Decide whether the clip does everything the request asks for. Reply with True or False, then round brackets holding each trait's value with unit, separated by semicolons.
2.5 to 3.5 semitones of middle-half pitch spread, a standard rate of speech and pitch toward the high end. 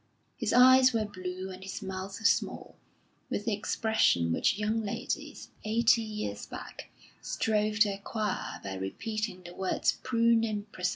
True (3.0 semitones; 150 wpm; 210 Hz)